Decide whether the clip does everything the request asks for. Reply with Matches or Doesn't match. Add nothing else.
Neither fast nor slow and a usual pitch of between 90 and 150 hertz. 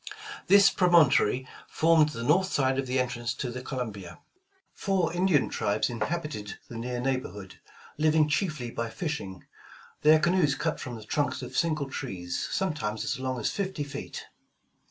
Matches